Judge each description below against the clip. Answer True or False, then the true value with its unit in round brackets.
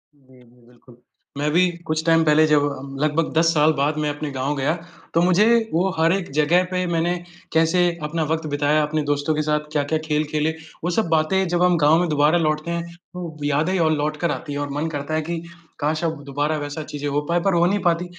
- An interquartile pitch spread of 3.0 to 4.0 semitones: False (2.4 semitones)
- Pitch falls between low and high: True (155 Hz)